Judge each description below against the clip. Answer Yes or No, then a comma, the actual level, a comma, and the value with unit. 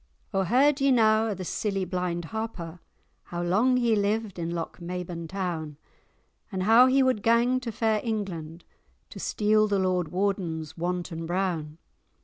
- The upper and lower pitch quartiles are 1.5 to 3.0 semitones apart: No, average, 4.4 semitones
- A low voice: No, high, 195 Hz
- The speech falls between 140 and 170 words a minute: Yes, average, 150 wpm